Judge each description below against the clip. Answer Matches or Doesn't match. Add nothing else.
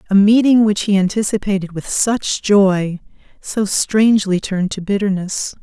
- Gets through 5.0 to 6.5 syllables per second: Doesn't match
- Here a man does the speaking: Doesn't match